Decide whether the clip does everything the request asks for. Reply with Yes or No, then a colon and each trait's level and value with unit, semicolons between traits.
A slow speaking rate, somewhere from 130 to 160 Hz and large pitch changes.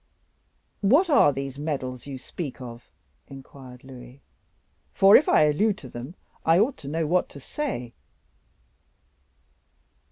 Yes: slow, 130 wpm; medium, 140 Hz; wide, 6.1 semitones